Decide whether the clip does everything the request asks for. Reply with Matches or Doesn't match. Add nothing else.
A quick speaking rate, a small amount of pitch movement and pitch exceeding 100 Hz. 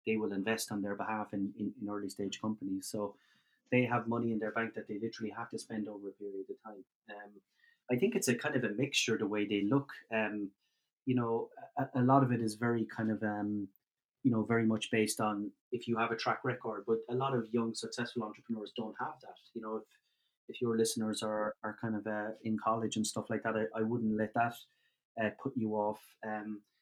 Matches